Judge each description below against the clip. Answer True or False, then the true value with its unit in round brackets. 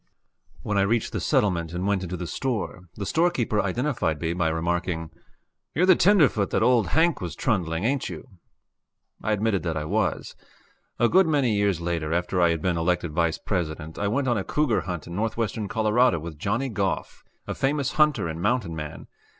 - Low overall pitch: True (100 Hz)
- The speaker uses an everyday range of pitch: False (6.2 semitones)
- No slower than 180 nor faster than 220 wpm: True (190 wpm)